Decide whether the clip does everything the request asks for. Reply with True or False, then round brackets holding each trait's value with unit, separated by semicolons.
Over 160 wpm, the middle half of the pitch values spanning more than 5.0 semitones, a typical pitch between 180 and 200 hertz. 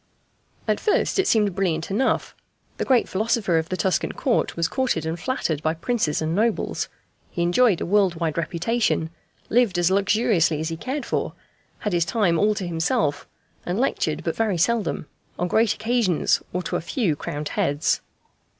True (175 wpm; 5.5 semitones; 185 Hz)